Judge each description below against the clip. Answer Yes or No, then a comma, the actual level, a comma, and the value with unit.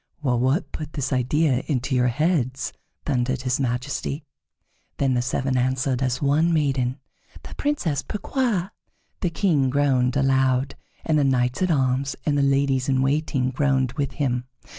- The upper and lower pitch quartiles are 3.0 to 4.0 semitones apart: No, narrow, 2.5 semitones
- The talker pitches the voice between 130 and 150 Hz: Yes, low, 135 Hz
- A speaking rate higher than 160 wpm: No, average, 155 wpm